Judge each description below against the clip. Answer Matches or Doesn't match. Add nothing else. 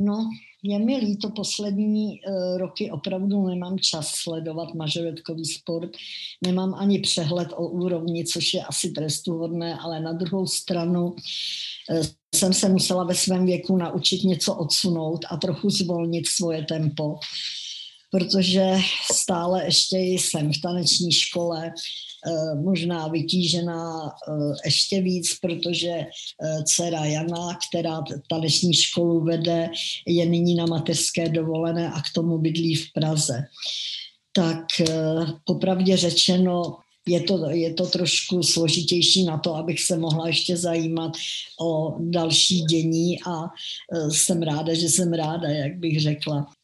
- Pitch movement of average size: Doesn't match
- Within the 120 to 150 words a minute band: Matches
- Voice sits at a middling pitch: Matches